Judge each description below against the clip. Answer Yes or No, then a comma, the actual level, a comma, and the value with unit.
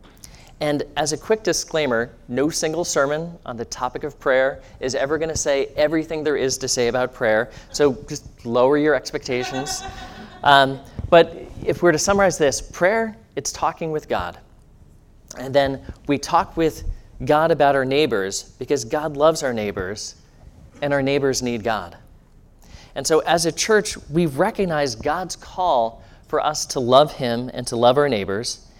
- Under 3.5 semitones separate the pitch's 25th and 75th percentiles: No, average, 4.0 semitones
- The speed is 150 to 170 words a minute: Yes, average, 165 wpm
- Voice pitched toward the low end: No, medium, 145 Hz